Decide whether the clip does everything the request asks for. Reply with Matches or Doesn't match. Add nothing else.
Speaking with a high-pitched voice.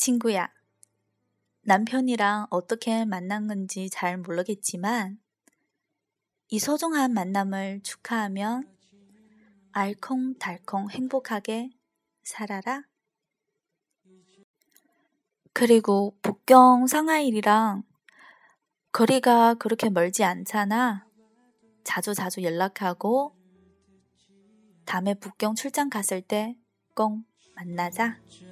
Matches